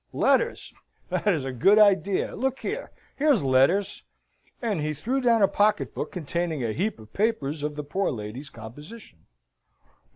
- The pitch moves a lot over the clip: Yes, wide, 7.6 semitones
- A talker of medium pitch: Yes, medium, 175 Hz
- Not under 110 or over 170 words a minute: Yes, average, 160 wpm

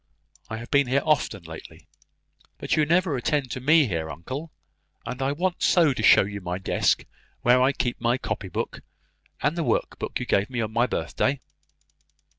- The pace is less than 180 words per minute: No, average, 190 wpm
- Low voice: Yes, low, 125 Hz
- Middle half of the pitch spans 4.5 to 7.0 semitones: Yes, average, 5.2 semitones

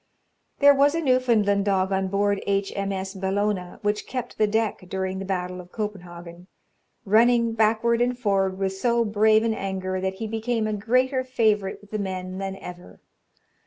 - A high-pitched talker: Yes, high, 205 Hz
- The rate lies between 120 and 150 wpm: No, average, 175 wpm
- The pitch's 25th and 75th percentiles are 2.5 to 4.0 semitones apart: Yes, average, 3.0 semitones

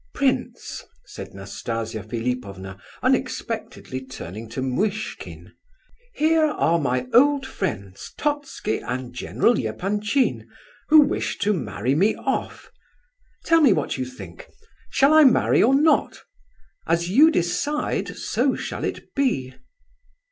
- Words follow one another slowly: Yes, slow, 120 wpm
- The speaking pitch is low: No, medium, 175 Hz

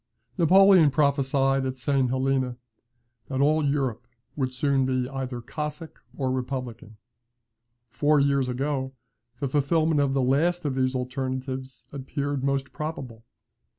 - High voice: No, low, 135 Hz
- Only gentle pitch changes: Yes, narrow, 2.0 semitones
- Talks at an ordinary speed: No, slow, 125 wpm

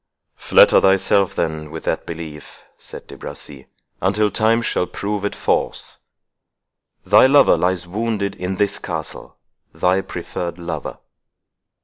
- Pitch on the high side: No, very low, 95 Hz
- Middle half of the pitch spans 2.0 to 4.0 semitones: Yes, average, 3.3 semitones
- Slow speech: Yes, slow, 120 wpm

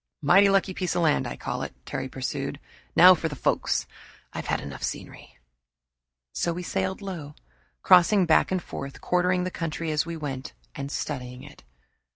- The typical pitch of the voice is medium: Yes, medium, 165 Hz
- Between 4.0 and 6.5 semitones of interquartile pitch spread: Yes, average, 4.3 semitones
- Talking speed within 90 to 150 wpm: No, average, 175 wpm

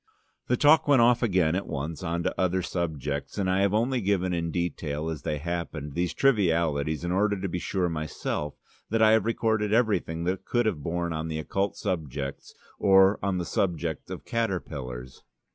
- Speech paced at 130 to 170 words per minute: No, average, 180 wpm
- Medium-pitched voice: No, very low, 90 Hz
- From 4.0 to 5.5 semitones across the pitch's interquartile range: Yes, average, 4.3 semitones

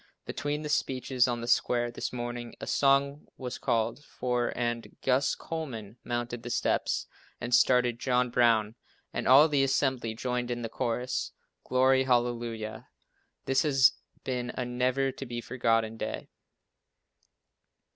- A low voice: Yes, low, 125 Hz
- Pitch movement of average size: No, narrow, 1.8 semitones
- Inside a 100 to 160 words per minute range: Yes, average, 140 wpm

